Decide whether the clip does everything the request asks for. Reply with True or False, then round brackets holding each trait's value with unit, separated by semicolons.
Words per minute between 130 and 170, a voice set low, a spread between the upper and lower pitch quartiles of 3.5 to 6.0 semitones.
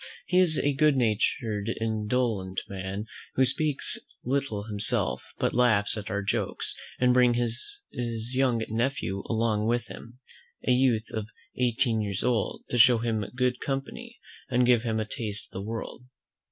False (155 wpm; 115 Hz; 2.9 semitones)